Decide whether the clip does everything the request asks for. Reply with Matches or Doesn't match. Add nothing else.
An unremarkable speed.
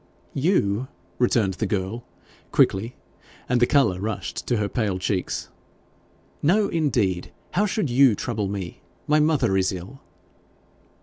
Doesn't match